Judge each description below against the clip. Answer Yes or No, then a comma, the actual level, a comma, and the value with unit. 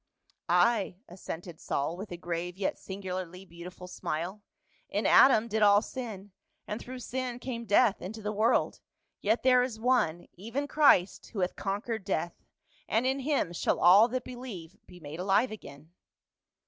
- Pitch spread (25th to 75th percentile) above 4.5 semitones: Yes, average, 5.0 semitones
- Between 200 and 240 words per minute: No, average, 160 wpm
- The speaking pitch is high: Yes, high, 205 Hz